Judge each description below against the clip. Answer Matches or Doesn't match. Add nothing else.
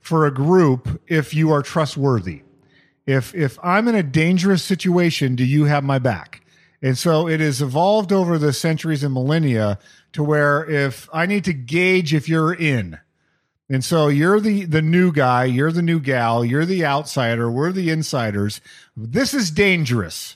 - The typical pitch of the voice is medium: Matches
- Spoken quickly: Doesn't match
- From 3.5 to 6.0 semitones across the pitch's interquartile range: Matches